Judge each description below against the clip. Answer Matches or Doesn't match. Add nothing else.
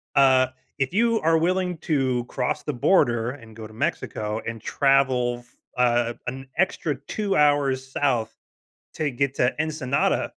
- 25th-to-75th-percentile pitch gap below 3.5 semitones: Doesn't match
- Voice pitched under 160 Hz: Matches